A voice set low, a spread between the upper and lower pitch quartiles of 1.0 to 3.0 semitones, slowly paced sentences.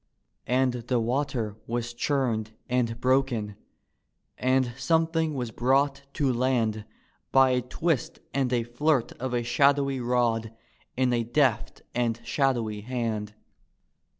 Yes: low, 125 Hz; narrow, 2.6 semitones; slow, 125 wpm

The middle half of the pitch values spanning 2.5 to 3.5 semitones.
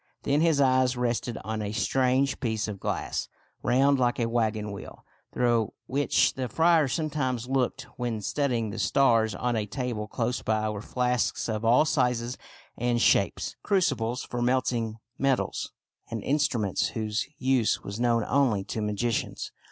Yes: average, 3.0 semitones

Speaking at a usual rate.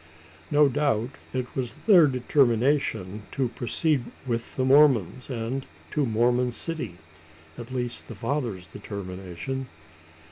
No: slow, 120 wpm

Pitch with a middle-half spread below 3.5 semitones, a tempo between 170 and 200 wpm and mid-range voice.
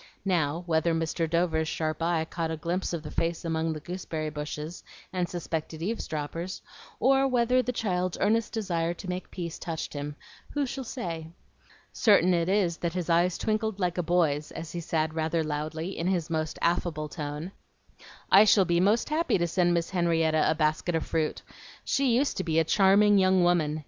Yes: average, 2.8 semitones; average, 185 wpm; medium, 170 Hz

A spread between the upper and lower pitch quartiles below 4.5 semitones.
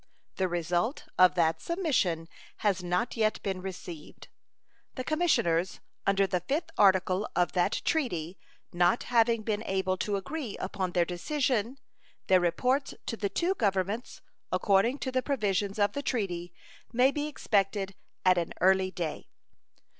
No: average, 5.3 semitones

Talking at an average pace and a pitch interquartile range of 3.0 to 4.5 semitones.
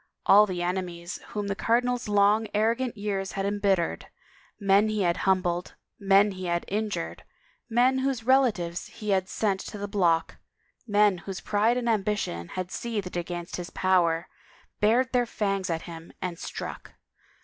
Yes: average, 160 wpm; average, 3.3 semitones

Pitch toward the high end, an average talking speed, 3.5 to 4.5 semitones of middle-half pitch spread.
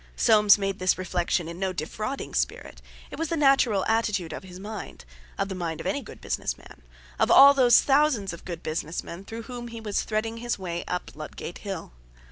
No: high, 195 Hz; average, 195 wpm; average, 5.0 semitones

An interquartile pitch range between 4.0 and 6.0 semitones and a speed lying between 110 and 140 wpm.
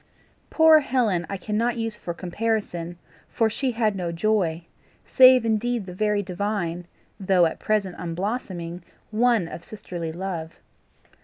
Yes: average, 4.5 semitones; slow, 135 wpm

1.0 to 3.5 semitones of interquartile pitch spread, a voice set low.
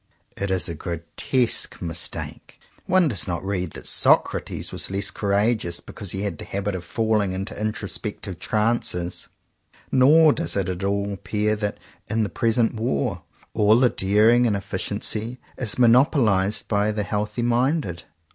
Yes: average, 3.1 semitones; low, 105 Hz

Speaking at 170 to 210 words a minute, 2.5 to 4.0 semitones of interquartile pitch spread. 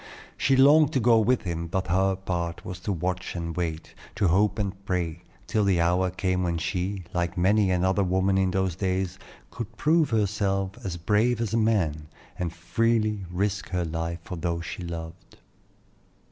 Yes: average, 175 wpm; average, 3.0 semitones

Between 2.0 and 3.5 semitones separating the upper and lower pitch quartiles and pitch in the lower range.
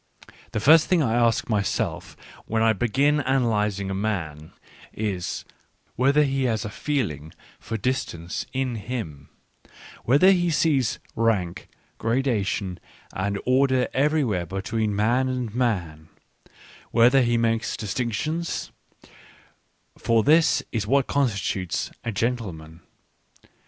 No: average, 4.7 semitones; low, 115 Hz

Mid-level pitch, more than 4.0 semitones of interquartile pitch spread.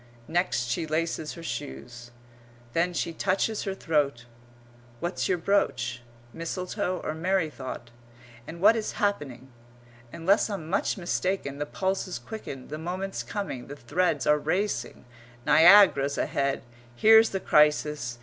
Yes: medium, 165 Hz; average, 5.2 semitones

